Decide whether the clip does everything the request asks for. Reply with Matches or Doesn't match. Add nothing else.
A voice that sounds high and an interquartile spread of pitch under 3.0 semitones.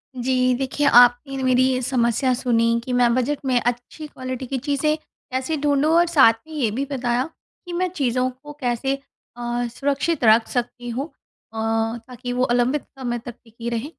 Matches